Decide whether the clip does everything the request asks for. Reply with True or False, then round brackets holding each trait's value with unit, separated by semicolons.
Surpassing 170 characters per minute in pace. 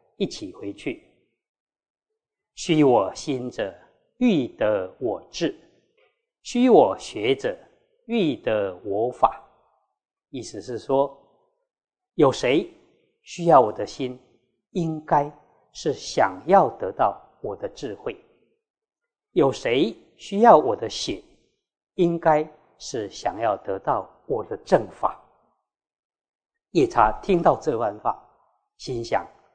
False (140 characters per minute)